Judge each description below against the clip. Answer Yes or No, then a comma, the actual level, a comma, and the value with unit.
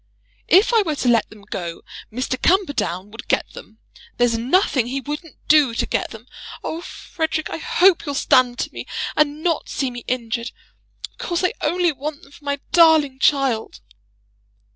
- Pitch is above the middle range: Yes, very high, 280 Hz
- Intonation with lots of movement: No, average, 4.9 semitones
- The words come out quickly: No, average, 175 wpm